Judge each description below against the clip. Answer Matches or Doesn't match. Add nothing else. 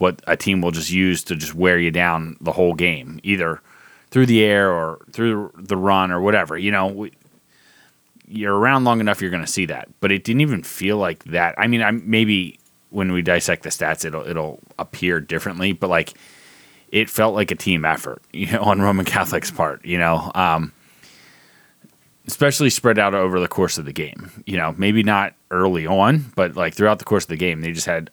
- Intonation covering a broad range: Doesn't match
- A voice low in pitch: Matches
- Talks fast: Matches